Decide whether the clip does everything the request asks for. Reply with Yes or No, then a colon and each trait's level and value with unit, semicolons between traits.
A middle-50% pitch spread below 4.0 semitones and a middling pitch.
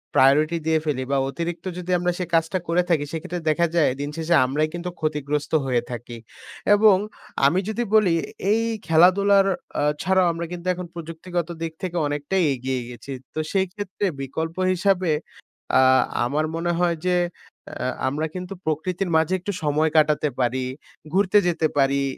Yes: average, 3.4 semitones; medium, 165 Hz